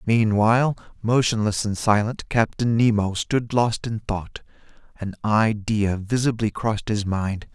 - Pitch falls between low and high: No, low, 110 Hz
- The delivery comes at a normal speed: No, slow, 125 wpm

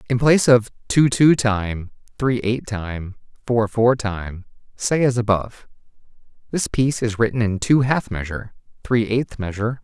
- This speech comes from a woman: No, male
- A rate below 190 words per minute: Yes, average, 175 wpm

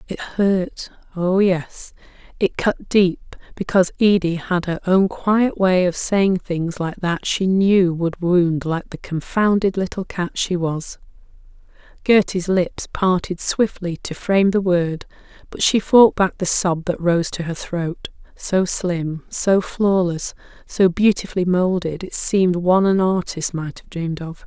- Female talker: Yes, female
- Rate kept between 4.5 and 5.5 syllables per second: No, 4.0 syllables/s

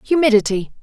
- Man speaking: No, female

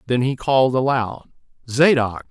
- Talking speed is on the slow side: Yes, slow, 130 wpm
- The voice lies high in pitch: No, low, 125 Hz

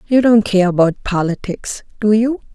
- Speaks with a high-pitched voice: Yes, high, 210 Hz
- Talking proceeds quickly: No, average, 165 wpm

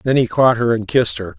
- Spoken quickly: Yes, fast, 305 wpm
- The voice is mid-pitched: No, low, 120 Hz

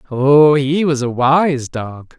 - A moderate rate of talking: Yes, average, 165 wpm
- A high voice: No, medium, 140 Hz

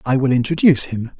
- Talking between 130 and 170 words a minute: No, average, 200 wpm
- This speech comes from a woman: No, male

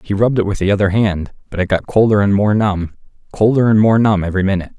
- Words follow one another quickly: Yes, fast, 250 wpm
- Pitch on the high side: No, low, 100 Hz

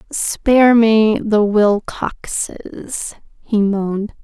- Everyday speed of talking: No, slow, 85 wpm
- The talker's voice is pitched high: Yes, high, 215 Hz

